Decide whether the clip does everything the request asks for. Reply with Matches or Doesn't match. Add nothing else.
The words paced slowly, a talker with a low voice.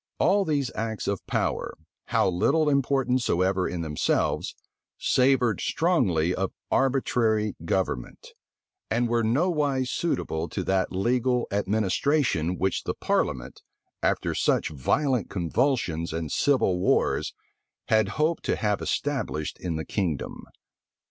Matches